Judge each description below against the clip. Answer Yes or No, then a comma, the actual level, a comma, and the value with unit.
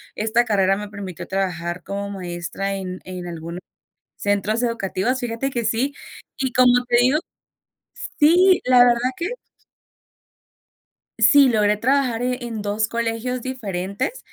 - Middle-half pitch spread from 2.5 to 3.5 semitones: No, average, 4.3 semitones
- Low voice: No, high, 225 Hz